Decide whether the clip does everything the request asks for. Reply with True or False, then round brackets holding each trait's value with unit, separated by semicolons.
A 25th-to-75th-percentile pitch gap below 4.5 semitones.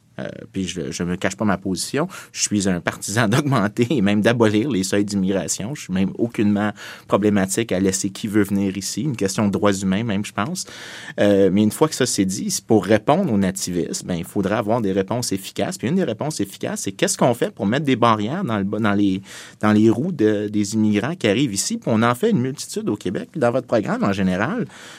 True (2.7 semitones)